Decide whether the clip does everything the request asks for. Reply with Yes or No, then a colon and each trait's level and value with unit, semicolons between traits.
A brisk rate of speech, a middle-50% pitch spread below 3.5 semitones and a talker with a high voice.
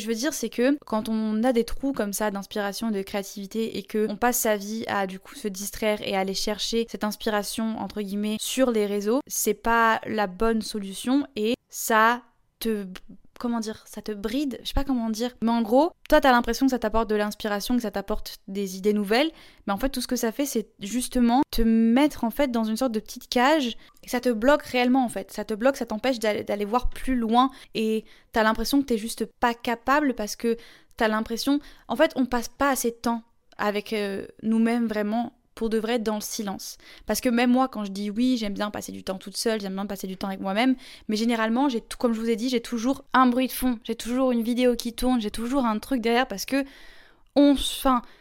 Yes: fast, 235 wpm; average, 2.9 semitones; high, 230 Hz